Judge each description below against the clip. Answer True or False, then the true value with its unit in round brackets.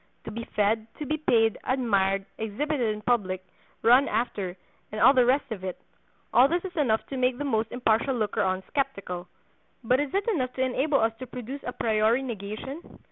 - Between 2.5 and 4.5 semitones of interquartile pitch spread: True (3.9 semitones)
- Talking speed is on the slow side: False (190 wpm)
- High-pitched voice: True (235 Hz)